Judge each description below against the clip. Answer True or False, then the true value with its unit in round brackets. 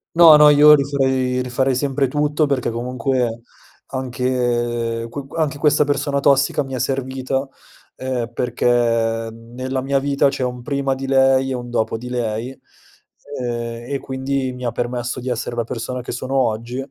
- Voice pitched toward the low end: True (130 Hz)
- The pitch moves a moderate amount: False (2.2 semitones)